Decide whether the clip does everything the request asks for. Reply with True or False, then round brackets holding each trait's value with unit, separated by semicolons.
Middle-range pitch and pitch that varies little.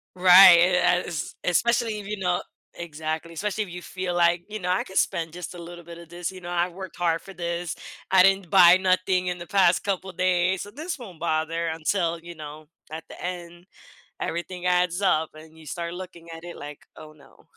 True (175 Hz; 1.7 semitones)